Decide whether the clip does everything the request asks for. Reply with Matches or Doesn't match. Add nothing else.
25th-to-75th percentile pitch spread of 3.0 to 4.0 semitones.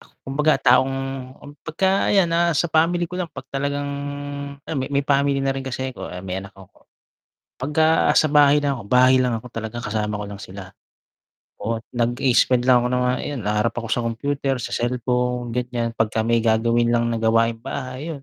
Matches